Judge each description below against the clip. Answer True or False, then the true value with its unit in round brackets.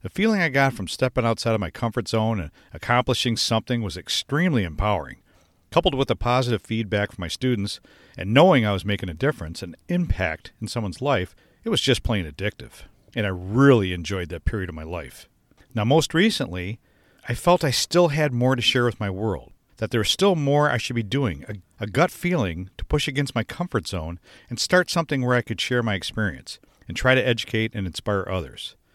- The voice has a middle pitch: False (115 Hz)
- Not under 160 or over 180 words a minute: False (205 wpm)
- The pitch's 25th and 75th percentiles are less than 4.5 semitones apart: False (5.4 semitones)